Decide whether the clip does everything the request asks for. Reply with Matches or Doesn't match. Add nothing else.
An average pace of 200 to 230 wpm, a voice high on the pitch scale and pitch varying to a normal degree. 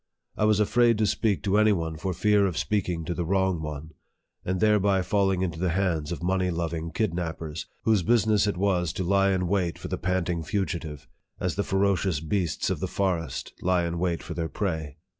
Doesn't match